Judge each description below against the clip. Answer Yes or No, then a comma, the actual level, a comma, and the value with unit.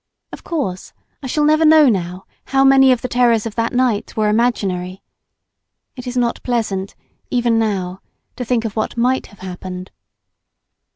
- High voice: Yes, high, 230 Hz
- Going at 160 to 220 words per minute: Yes, average, 165 wpm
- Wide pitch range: No, average, 4.5 semitones